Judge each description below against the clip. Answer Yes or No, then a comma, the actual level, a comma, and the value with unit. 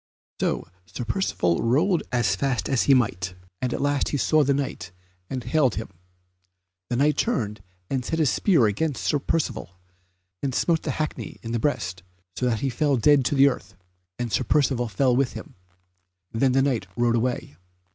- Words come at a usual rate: Yes, average, 185 wpm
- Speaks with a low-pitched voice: Yes, low, 130 Hz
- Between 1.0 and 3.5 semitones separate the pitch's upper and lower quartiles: No, average, 3.9 semitones